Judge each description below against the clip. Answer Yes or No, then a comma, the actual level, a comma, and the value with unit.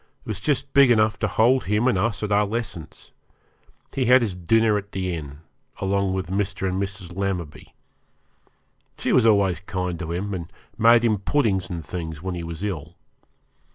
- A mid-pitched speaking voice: No, low, 100 Hz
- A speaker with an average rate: Yes, average, 185 wpm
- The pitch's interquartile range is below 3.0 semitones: No, average, 3.6 semitones